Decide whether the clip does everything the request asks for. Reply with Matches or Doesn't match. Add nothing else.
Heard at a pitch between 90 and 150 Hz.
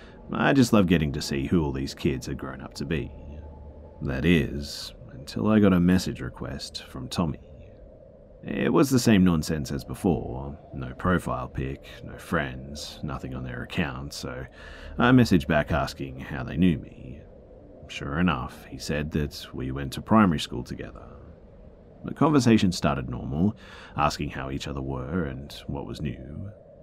Doesn't match